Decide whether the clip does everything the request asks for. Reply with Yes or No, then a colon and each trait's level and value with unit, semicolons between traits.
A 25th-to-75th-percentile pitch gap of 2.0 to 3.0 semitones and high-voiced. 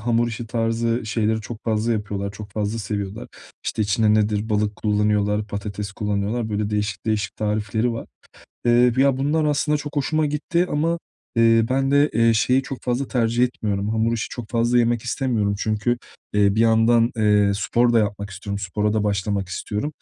No: narrow, 2.6 semitones; low, 110 Hz